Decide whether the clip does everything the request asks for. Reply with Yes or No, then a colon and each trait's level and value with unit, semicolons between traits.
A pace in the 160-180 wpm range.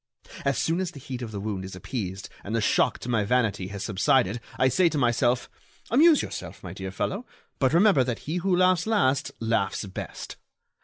No: average, 200 wpm